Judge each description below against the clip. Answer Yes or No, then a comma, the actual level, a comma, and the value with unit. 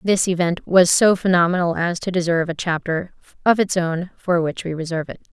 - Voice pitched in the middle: Yes, medium, 175 Hz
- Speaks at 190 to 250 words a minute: Yes, average, 200 wpm